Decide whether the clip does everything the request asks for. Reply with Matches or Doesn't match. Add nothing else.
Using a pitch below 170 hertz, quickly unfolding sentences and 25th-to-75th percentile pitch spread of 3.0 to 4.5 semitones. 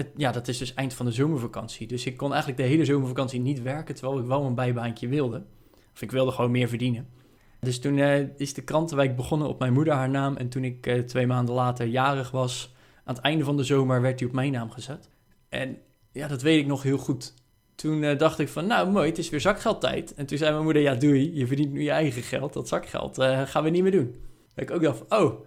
Doesn't match